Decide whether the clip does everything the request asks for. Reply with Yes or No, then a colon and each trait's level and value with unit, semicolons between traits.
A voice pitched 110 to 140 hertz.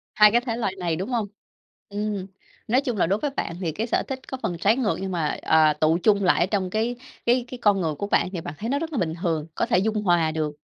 No: high, 200 Hz